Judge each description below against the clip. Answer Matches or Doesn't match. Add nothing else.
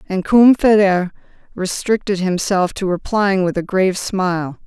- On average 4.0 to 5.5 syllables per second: Matches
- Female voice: Matches